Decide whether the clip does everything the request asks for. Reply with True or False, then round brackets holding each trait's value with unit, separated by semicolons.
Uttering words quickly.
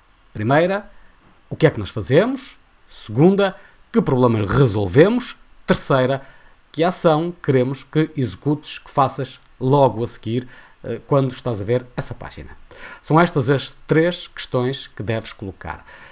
False (135 wpm)